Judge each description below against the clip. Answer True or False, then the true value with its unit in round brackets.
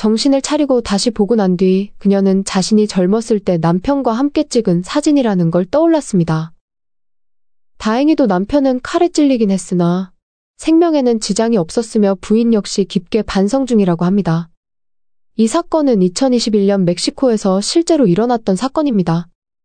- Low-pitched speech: False (215 Hz)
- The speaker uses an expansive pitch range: True (5.9 semitones)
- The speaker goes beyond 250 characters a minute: True (320 characters per minute)